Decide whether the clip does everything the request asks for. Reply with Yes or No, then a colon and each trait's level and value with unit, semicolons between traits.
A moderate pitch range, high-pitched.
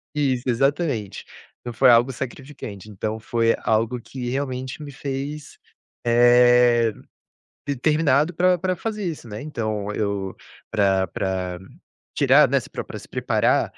No: average, 4.6 semitones; low, 125 Hz